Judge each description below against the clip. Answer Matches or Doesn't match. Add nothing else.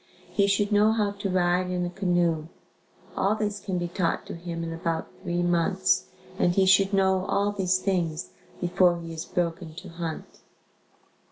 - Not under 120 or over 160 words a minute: Doesn't match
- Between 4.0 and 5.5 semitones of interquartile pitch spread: Doesn't match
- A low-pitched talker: Doesn't match